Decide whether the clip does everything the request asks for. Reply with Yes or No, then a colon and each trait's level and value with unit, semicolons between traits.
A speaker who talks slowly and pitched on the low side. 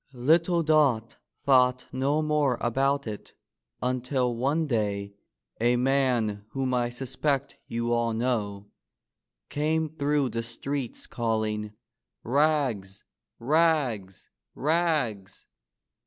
Yes: slow, 95 wpm; low, 125 Hz